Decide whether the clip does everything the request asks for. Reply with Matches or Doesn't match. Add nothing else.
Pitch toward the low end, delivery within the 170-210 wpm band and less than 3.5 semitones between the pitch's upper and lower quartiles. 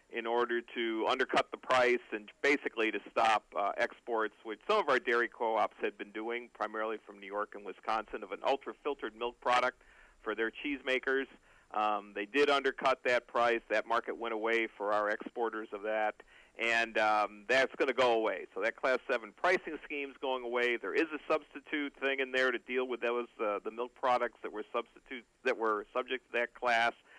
Matches